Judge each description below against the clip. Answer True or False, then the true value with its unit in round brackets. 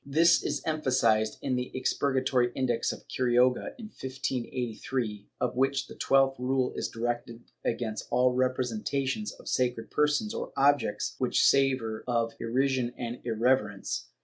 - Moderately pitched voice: False (125 Hz)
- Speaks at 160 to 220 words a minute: False (140 wpm)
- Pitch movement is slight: True (2.3 semitones)